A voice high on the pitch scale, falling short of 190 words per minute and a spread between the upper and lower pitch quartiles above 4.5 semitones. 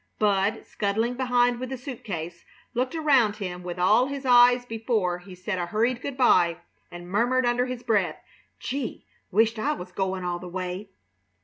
Yes: high, 220 Hz; average, 180 wpm; wide, 5.4 semitones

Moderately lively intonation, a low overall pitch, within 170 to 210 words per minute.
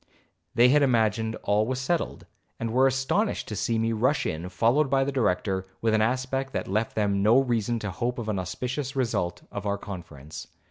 Yes: average, 4.2 semitones; low, 115 Hz; average, 195 wpm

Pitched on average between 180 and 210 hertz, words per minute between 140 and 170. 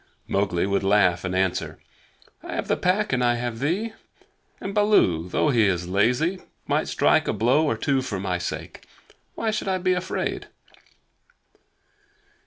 No: low, 120 Hz; average, 165 wpm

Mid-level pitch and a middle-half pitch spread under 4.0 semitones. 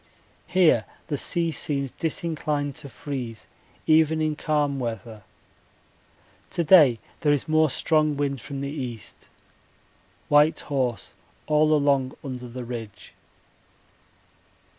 Yes: medium, 145 Hz; average, 3.4 semitones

